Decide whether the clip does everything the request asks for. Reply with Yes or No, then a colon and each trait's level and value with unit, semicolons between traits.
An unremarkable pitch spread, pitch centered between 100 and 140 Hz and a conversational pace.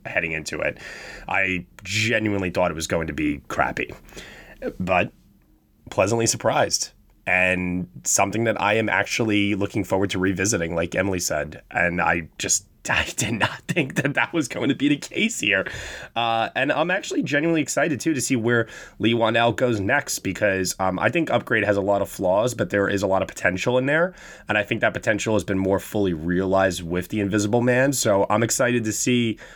Yes: average, 3.9 semitones; low, 105 Hz; average, 195 wpm